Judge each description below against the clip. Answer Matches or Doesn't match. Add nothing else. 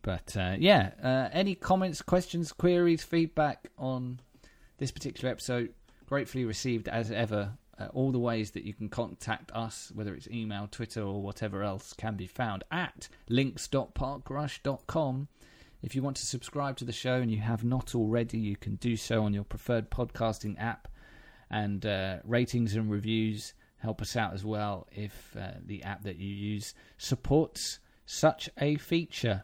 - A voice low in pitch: Matches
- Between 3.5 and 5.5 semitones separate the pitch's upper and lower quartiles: Matches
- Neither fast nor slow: Matches